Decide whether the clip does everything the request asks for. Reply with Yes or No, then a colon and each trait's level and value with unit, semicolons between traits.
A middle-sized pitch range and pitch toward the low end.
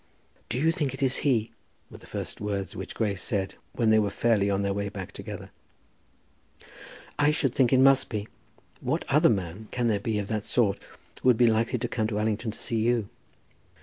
Yes: average, 3.7 semitones; low, 110 Hz